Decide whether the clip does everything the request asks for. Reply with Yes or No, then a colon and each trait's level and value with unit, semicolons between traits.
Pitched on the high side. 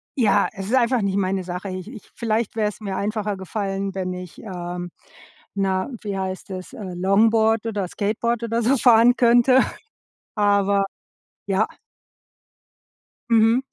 Yes: high, 205 Hz